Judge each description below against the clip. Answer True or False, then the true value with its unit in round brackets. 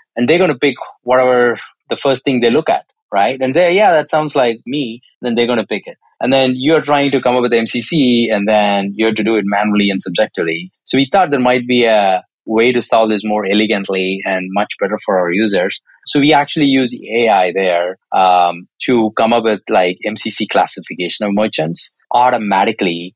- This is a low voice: True (115 Hz)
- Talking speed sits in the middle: False (210 wpm)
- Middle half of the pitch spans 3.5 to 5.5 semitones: True (4.1 semitones)